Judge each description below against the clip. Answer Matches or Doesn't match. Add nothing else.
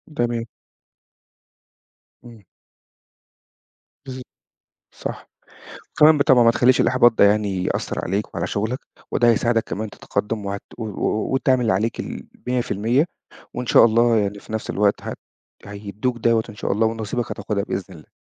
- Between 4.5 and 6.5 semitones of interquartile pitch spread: Doesn't match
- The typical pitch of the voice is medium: Doesn't match